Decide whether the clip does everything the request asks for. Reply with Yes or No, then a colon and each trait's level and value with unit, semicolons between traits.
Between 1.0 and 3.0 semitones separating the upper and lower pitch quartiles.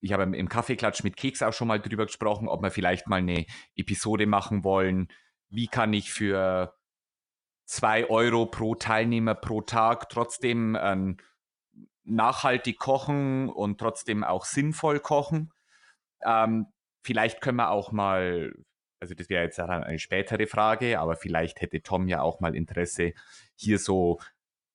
No: average, 3.8 semitones